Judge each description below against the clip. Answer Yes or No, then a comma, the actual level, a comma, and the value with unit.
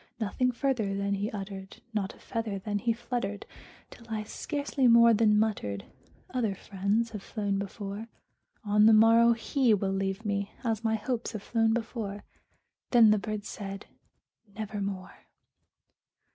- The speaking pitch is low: No, high, 215 Hz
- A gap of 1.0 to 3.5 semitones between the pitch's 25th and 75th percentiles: Yes, narrow, 2.5 semitones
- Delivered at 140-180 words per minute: Yes, average, 145 wpm